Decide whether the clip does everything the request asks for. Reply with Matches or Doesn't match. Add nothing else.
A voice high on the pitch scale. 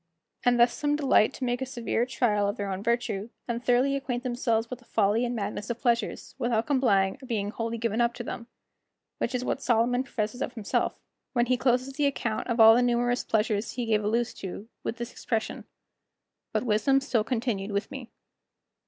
Matches